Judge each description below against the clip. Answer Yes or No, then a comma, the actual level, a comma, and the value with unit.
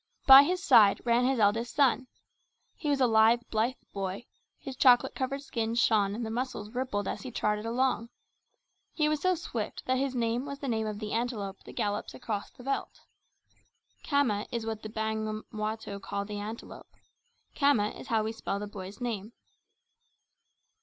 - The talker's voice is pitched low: No, high, 230 Hz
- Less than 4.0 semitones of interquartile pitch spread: Yes, average, 3.5 semitones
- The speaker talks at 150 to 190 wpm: Yes, average, 175 wpm